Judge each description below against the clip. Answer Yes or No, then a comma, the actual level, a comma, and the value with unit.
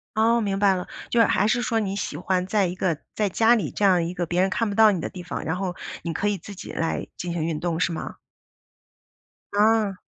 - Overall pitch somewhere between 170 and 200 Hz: Yes, high, 190 Hz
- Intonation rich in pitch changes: No, average, 3.4 semitones